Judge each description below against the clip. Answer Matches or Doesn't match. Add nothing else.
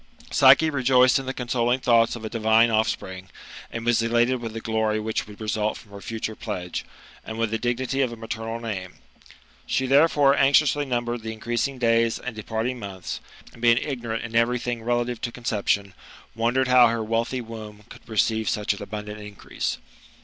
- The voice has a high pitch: Doesn't match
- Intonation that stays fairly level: Matches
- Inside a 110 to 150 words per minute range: Doesn't match